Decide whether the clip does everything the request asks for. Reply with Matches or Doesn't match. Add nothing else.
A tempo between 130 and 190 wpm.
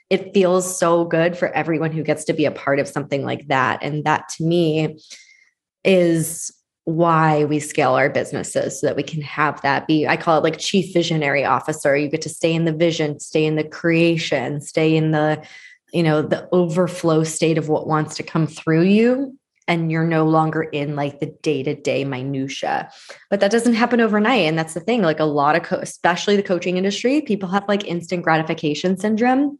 Doesn't match